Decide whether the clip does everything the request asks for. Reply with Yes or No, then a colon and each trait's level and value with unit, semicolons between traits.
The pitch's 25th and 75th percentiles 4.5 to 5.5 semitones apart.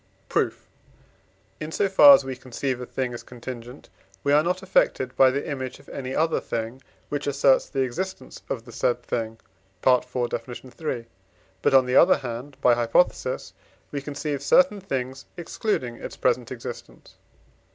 No: average, 3.1 semitones